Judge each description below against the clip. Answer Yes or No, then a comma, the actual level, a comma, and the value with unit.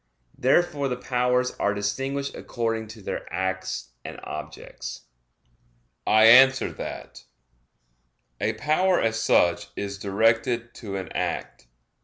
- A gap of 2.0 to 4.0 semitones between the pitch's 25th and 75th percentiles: No, average, 4.5 semitones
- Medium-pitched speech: No, low, 115 Hz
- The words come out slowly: Yes, slow, 115 wpm